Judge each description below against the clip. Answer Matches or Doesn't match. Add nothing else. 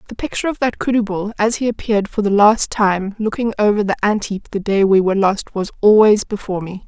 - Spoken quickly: Matches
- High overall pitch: Matches